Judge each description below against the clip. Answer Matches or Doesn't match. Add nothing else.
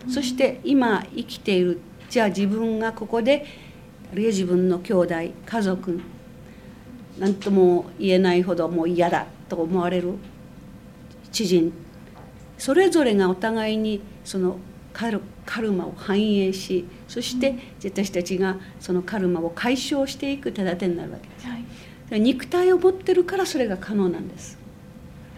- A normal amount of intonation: Matches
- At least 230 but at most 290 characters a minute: Matches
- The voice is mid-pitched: Doesn't match